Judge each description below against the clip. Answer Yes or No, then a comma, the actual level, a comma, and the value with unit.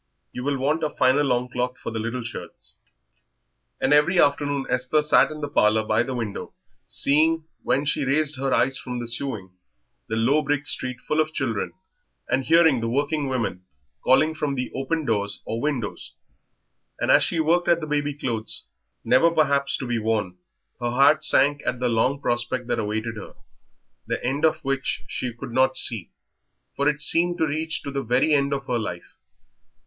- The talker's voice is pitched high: No, low, 135 Hz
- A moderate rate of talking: Yes, average, 185 wpm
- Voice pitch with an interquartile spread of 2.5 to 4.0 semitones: Yes, average, 3.7 semitones